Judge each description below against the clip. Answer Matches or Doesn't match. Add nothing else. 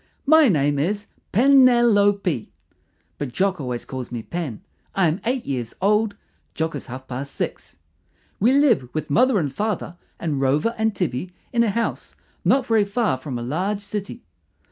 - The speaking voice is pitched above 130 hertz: Matches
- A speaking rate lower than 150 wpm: Doesn't match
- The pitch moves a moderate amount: Doesn't match